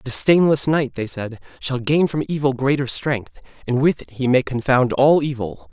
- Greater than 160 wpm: Yes, average, 200 wpm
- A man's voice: Yes, male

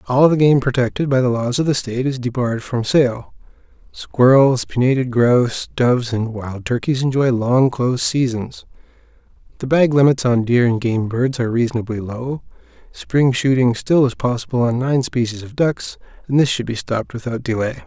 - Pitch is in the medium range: No, low, 125 Hz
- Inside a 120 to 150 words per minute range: No, average, 180 wpm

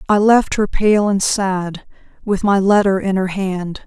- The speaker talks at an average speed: Yes, average, 185 wpm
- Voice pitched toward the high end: Yes, high, 195 Hz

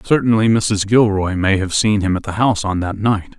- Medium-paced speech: No, fast, 230 wpm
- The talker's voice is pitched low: Yes, low, 100 Hz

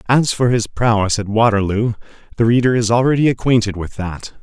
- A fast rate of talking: No, average, 175 wpm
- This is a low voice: Yes, low, 115 Hz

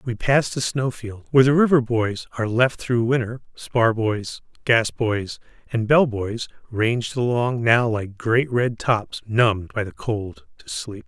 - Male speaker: Yes, male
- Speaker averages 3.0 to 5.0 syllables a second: Yes, 4.2 syllables/s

